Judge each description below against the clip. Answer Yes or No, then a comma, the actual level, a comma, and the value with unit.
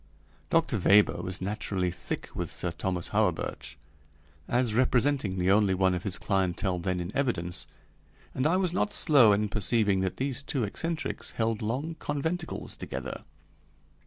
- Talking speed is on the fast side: No, average, 150 wpm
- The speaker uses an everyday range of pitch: No, wide, 6.7 semitones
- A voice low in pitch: Yes, low, 105 Hz